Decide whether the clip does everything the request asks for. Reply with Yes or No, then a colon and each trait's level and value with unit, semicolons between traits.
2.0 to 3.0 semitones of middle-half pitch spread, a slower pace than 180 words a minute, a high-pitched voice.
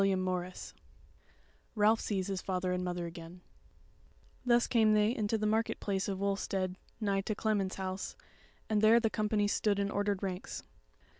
Yes: narrow, 2.4 semitones; average, 160 wpm; high, 200 Hz